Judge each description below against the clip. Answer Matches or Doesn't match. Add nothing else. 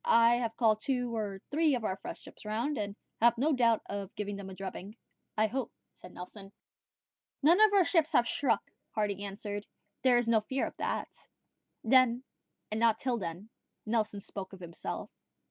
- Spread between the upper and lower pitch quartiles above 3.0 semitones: Matches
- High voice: Matches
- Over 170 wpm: Matches